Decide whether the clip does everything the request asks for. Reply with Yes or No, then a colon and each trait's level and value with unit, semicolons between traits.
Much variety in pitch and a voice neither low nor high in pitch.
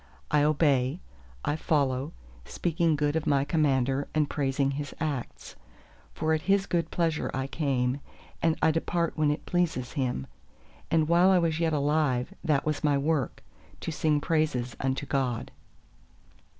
No: average, 3.0 semitones; medium, 150 Hz